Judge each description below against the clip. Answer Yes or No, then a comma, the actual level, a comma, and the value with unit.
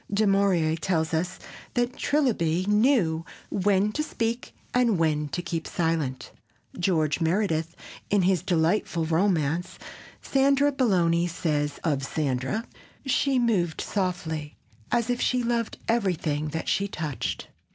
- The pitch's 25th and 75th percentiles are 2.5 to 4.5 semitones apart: No, average, 5.3 semitones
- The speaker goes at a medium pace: No, slow, 125 wpm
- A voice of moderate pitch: Yes, medium, 180 Hz